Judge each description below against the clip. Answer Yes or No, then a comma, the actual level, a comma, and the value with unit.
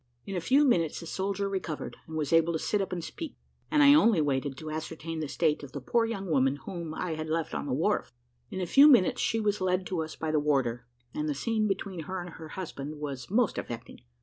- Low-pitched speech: No, medium, 165 Hz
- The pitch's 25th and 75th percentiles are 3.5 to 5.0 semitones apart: Yes, average, 4.6 semitones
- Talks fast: Yes, fast, 245 wpm